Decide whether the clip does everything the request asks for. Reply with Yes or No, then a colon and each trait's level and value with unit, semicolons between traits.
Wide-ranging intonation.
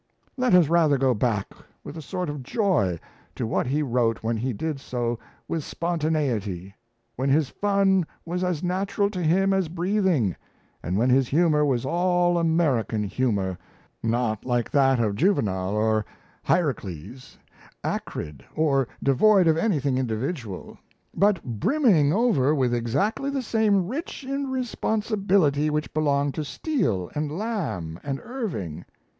Yes: wide, 7.6 semitones